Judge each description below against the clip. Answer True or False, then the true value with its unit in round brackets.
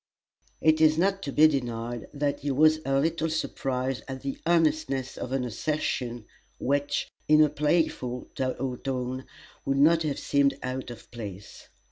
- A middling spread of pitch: True (3.4 semitones)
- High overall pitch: False (135 Hz)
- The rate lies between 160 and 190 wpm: False (150 wpm)